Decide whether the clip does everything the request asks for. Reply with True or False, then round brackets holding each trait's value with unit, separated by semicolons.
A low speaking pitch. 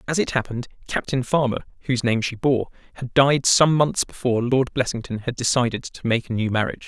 True (125 Hz)